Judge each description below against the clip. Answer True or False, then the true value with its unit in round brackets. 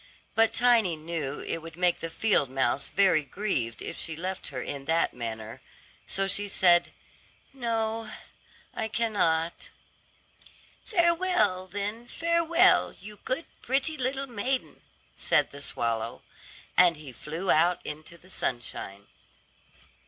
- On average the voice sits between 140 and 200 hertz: True (185 Hz)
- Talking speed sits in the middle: False (125 wpm)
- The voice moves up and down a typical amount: False (6.8 semitones)